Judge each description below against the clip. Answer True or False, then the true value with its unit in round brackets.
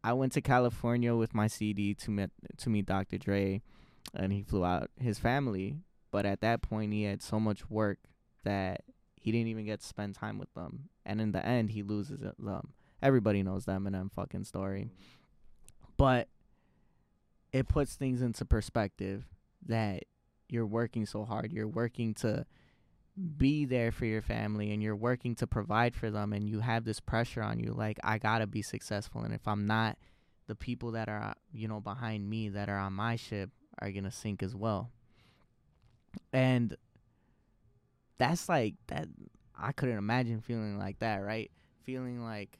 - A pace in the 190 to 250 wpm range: False (180 wpm)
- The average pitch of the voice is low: True (110 Hz)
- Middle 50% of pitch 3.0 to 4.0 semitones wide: False (2.5 semitones)